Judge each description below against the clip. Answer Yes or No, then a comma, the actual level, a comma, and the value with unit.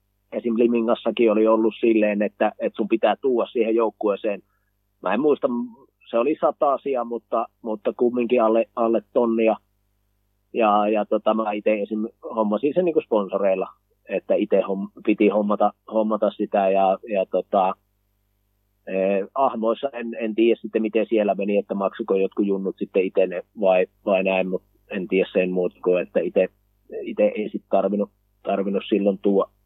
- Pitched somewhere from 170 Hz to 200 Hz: No, low, 105 Hz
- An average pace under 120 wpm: No, average, 150 wpm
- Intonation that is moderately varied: No, narrow, 2.1 semitones